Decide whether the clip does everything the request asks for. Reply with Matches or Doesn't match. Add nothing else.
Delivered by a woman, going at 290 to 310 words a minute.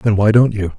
Doesn't match